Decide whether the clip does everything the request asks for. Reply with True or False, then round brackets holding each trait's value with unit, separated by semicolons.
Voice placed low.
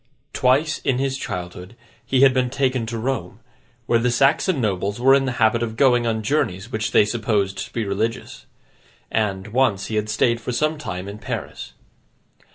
True (115 Hz)